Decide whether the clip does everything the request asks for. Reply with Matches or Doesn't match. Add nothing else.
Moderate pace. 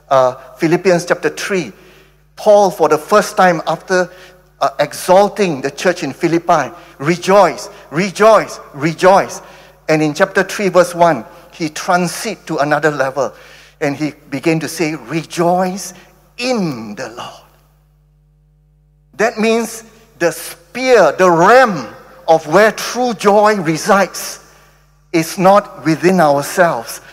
Doesn't match